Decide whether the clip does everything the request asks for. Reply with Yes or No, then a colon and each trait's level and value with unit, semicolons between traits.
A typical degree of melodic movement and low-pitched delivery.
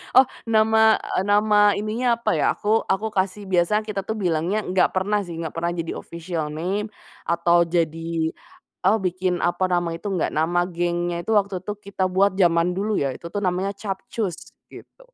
No: average, 3.3 semitones; medium, 185 Hz